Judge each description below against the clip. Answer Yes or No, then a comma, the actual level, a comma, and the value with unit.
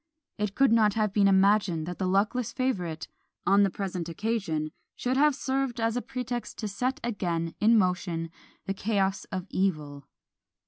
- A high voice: Yes, high, 200 Hz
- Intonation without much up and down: No, average, 4.3 semitones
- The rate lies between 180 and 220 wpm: No, average, 165 wpm